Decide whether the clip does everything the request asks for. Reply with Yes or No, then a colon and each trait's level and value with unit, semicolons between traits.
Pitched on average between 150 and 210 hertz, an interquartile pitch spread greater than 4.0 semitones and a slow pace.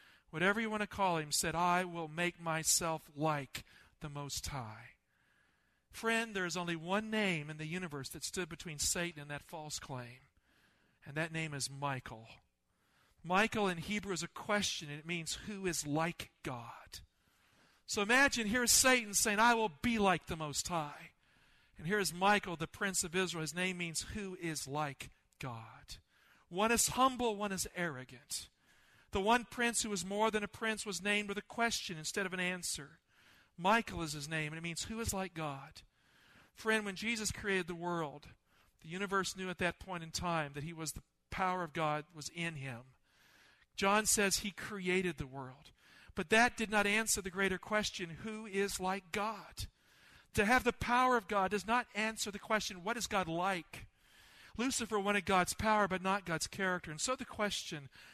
No: medium, 185 Hz; average, 4.7 semitones; average, 185 wpm